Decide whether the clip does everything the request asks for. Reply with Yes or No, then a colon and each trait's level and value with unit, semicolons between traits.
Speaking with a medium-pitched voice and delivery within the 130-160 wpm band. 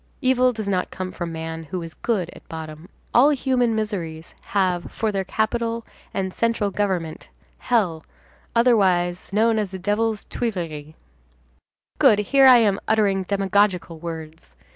No: high, 195 Hz; average, 140 wpm